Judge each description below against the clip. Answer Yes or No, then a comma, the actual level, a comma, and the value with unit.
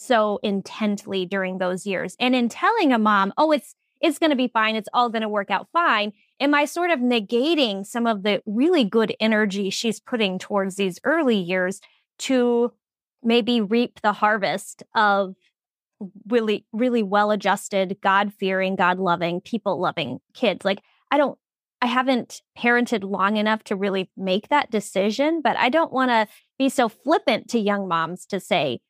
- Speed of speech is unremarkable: Yes, average, 165 wpm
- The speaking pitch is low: No, high, 215 Hz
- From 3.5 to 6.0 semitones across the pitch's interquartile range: Yes, average, 4.1 semitones